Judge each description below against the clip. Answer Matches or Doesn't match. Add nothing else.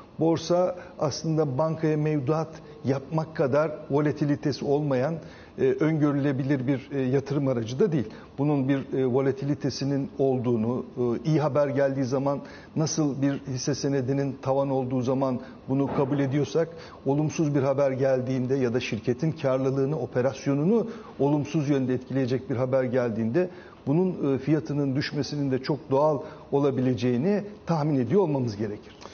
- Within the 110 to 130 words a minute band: Matches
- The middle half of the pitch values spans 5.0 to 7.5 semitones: Doesn't match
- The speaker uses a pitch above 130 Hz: Matches